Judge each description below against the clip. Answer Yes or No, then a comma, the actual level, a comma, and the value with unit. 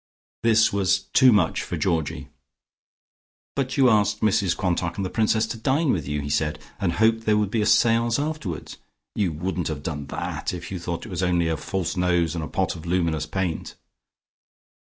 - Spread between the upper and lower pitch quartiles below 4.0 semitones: No, average, 4.9 semitones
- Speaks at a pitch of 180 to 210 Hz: No, very low, 95 Hz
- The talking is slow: No, average, 195 wpm